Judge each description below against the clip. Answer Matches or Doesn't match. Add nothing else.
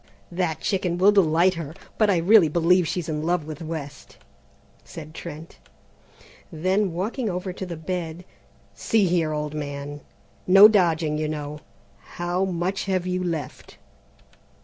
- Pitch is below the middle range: Doesn't match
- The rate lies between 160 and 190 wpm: Doesn't match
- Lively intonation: Doesn't match